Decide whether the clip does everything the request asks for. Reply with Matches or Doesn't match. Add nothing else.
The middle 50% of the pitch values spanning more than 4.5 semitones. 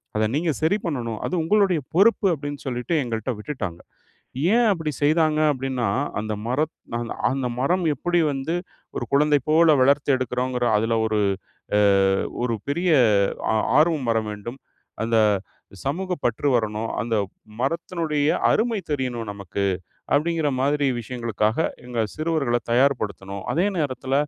Matches